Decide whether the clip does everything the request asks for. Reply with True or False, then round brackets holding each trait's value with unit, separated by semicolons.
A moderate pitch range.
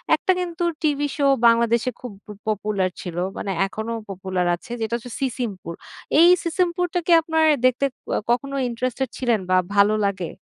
False (6.4 semitones)